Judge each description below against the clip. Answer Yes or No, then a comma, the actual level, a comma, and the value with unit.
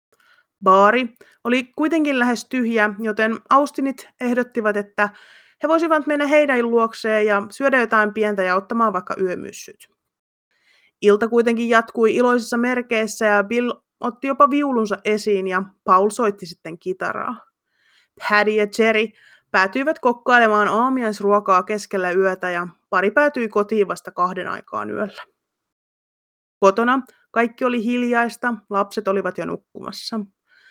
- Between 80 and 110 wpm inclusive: No, average, 120 wpm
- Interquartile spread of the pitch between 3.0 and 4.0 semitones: Yes, average, 3.3 semitones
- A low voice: No, high, 225 Hz